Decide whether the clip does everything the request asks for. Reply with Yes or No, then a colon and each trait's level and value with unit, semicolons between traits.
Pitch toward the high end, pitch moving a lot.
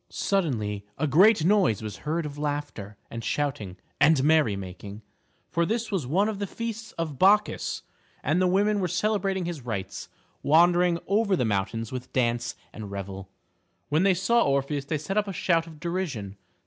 No: medium, 155 Hz; wide, 8.4 semitones